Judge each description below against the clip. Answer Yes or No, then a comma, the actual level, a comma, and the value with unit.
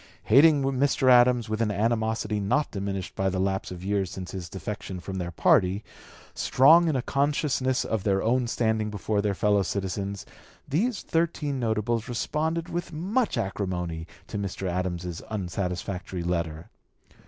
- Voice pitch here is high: No, low, 105 Hz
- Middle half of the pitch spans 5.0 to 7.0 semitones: Yes, wide, 5.6 semitones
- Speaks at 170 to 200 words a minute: No, average, 150 wpm